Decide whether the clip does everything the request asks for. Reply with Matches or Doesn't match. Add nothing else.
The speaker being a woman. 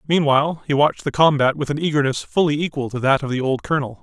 Doesn't match